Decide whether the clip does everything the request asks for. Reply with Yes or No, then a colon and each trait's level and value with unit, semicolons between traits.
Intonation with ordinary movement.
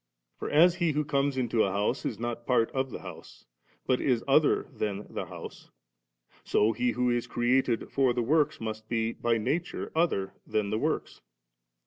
Yes: average, 3.7 semitones